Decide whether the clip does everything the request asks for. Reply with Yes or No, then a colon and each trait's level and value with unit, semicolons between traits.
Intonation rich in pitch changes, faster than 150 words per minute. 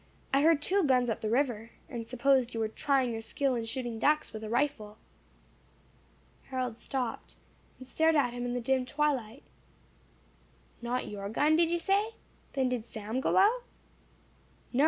No: average, 4.1 semitones; average, 170 wpm